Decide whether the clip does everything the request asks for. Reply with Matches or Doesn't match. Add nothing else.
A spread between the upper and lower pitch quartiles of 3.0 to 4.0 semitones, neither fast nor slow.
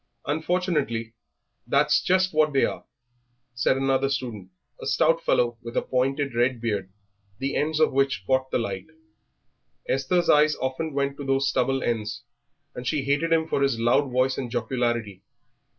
Matches